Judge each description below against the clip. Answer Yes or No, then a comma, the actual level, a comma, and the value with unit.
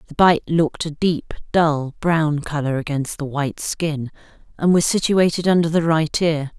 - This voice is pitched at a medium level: Yes, medium, 155 Hz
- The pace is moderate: Yes, average, 175 wpm